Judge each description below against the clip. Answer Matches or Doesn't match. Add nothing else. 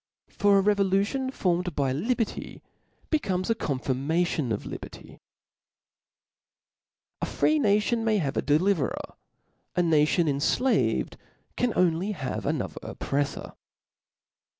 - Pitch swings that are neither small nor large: Doesn't match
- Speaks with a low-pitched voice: Doesn't match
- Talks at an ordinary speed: Doesn't match